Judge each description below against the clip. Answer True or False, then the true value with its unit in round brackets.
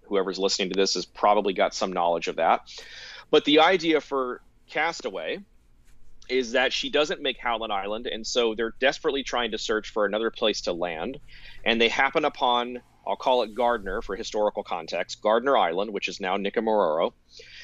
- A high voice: False (115 Hz)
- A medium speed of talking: True (175 wpm)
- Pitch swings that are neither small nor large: False (6.1 semitones)